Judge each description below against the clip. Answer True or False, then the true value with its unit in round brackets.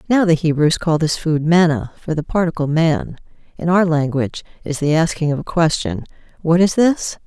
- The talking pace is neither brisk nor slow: True (190 wpm)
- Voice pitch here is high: False (160 Hz)